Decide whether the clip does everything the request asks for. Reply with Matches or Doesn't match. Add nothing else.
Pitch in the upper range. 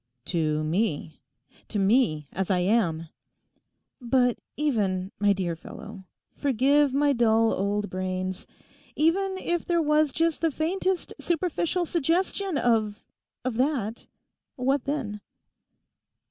Matches